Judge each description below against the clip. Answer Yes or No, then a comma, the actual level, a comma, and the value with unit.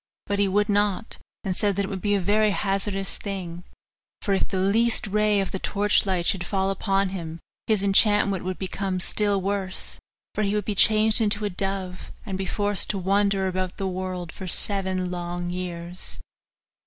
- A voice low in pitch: No, high, 195 Hz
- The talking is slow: No, average, 190 wpm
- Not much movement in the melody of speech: Yes, narrow, 1.7 semitones